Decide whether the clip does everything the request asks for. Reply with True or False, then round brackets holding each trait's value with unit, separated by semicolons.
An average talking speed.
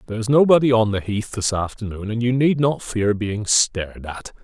False (215 wpm)